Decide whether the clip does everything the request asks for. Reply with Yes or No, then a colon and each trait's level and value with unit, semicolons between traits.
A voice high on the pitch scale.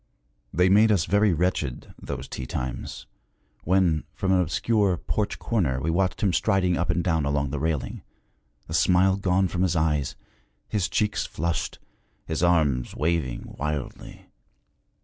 No: very low, 85 Hz